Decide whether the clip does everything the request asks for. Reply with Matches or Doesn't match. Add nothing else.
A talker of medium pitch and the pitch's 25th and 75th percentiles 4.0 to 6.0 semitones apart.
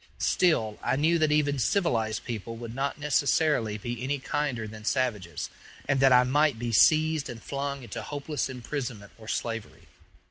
Doesn't match